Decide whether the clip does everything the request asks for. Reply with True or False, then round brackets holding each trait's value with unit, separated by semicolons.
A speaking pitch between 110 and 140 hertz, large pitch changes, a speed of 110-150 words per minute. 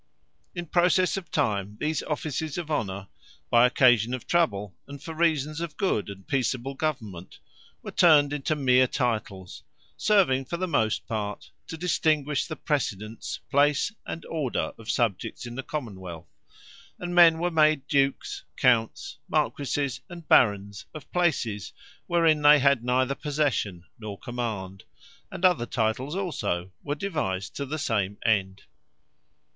True (135 Hz; 6.2 semitones; 145 wpm)